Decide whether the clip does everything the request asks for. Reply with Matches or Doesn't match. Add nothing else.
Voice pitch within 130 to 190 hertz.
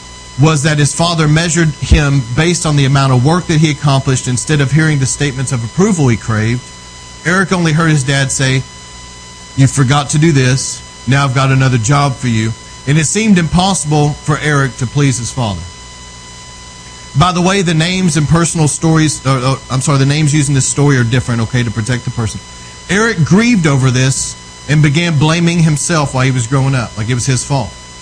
Matches